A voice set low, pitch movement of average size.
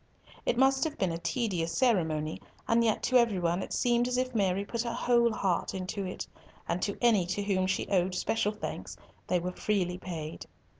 No: high, 200 Hz; average, 4.7 semitones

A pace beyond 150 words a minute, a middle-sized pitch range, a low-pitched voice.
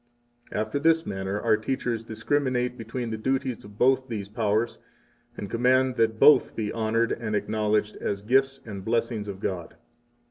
Yes: average, 165 wpm; average, 3.2 semitones; low, 115 Hz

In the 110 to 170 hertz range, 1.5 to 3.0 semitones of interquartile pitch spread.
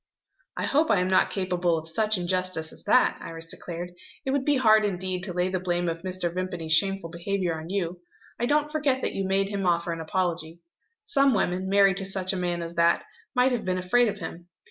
No: medium, 185 Hz; narrow, 2.6 semitones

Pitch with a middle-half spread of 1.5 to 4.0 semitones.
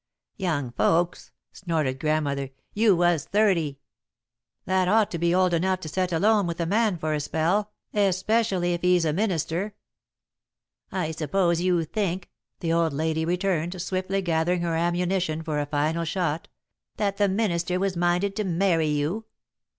Yes: average, 3.0 semitones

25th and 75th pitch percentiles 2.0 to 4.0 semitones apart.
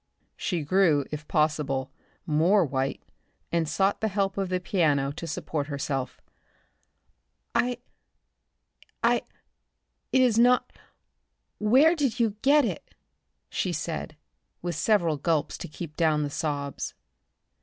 No: wide, 5.5 semitones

